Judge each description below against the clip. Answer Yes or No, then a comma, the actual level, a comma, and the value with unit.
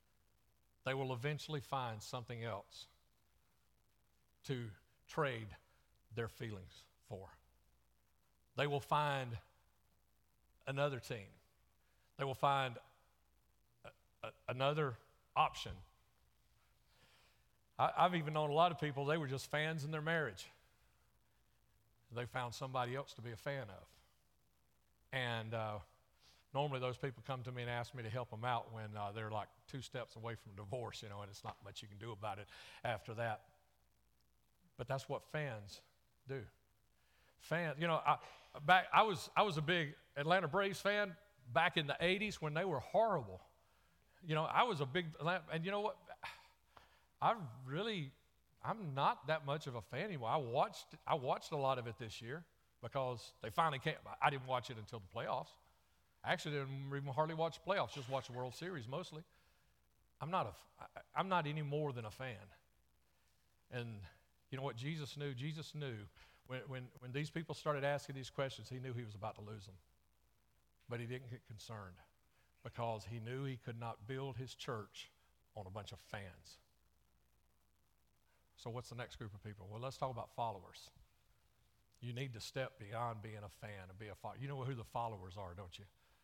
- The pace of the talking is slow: No, average, 175 wpm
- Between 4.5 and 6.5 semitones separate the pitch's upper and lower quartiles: Yes, average, 5.1 semitones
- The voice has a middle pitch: No, low, 125 Hz